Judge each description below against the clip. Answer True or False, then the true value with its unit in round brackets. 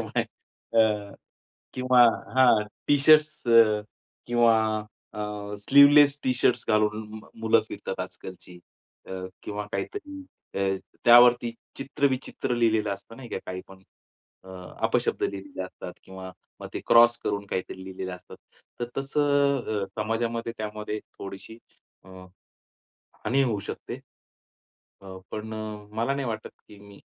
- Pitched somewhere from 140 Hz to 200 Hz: False (110 Hz)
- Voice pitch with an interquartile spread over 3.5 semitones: True (3.9 semitones)